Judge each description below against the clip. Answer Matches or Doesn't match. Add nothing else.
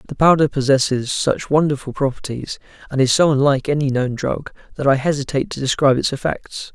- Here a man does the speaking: Matches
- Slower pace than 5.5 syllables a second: Doesn't match